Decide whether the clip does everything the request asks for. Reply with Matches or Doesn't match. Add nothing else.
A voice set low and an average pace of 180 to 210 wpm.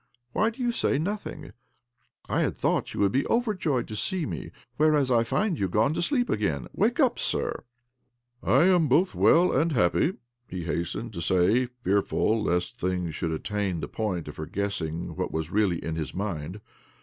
Matches